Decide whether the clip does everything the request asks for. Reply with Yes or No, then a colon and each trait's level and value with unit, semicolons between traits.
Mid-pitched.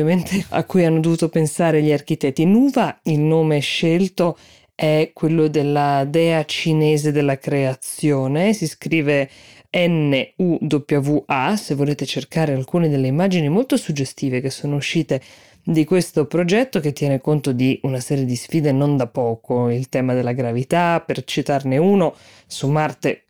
Yes: medium, 150 Hz